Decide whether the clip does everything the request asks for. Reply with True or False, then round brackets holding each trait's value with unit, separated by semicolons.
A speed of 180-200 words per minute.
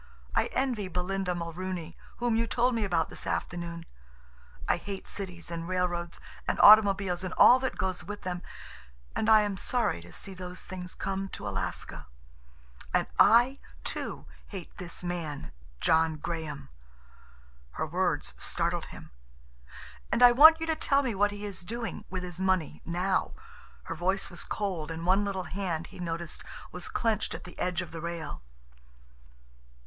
False (155 wpm)